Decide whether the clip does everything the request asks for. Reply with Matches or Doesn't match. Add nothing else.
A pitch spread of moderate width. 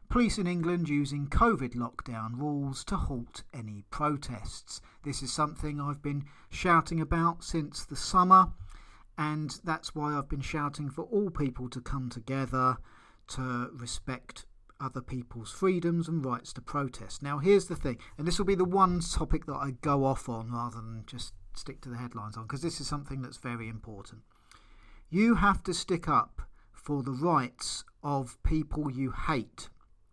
Matches